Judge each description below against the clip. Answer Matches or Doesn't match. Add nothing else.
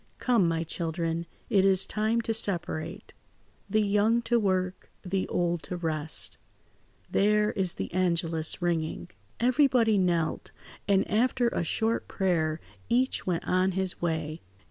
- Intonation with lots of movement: Doesn't match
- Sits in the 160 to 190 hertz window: Matches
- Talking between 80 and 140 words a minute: Matches